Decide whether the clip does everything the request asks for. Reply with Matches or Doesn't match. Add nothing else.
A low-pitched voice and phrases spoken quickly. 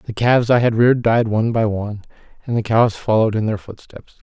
Matches